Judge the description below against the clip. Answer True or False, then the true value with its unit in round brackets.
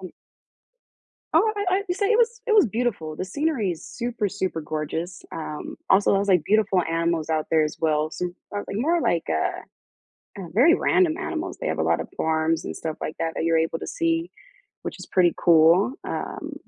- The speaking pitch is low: False (190 Hz)